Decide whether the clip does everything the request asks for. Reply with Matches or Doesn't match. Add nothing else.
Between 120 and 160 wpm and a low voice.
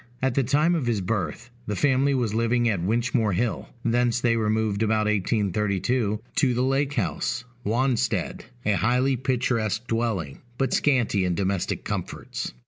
Matches